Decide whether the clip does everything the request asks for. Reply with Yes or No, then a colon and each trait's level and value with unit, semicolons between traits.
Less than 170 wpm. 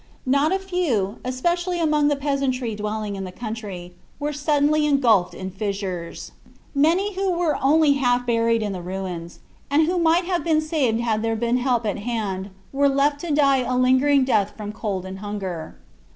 No: average, 180 wpm